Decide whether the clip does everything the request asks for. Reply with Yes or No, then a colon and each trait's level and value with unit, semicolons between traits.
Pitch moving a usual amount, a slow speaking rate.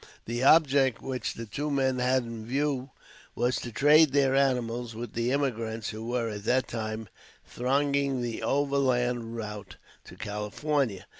No: average, 3.3 semitones; average, 150 wpm